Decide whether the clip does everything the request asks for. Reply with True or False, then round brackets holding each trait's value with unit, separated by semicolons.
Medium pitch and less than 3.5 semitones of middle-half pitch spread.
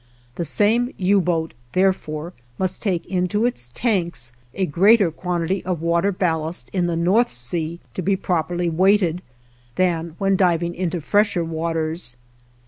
True (175 Hz; 2.7 semitones)